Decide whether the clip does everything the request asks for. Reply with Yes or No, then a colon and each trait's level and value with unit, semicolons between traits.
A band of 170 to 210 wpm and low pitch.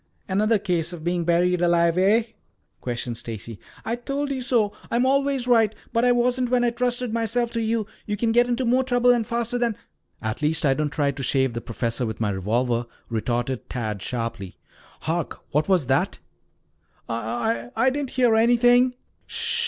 No: average, 185 wpm; high, 205 Hz